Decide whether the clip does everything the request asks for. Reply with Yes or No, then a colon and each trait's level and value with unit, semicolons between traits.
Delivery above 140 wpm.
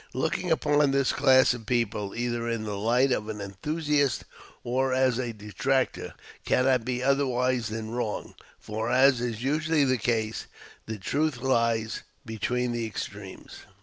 Yes: average, 150 wpm